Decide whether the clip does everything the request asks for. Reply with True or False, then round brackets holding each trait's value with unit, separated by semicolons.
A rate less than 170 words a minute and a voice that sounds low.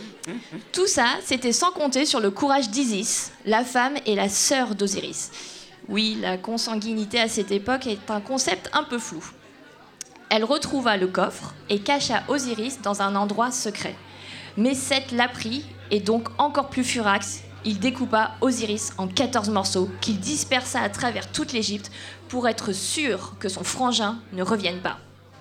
False (160 wpm; 225 Hz)